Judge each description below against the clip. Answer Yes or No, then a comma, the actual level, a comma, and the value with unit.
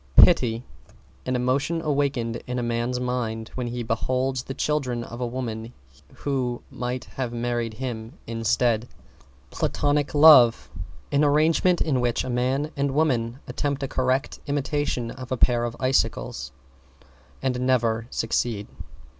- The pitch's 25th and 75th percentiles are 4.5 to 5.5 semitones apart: No, narrow, 2.6 semitones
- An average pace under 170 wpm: Yes, average, 140 wpm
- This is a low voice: Yes, low, 125 Hz